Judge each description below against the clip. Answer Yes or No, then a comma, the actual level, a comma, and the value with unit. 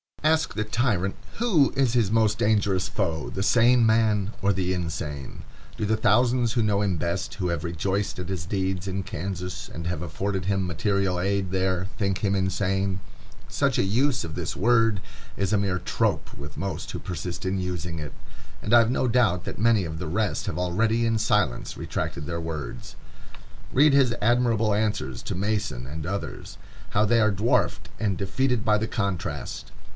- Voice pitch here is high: No, low, 100 Hz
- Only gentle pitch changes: No, average, 3.6 semitones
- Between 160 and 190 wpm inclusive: Yes, average, 180 wpm